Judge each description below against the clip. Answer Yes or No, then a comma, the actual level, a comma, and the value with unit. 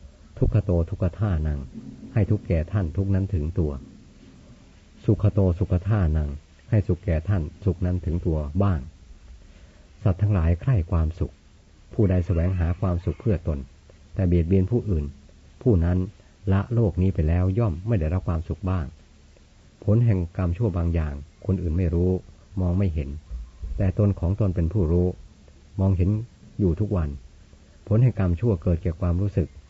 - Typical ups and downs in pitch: Yes, average, 3.9 semitones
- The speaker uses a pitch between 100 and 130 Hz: No, very low, 90 Hz